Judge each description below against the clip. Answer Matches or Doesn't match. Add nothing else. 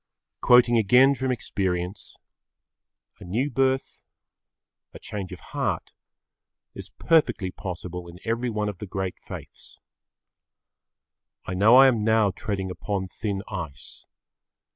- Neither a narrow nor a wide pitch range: Matches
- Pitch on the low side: Matches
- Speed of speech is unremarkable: Doesn't match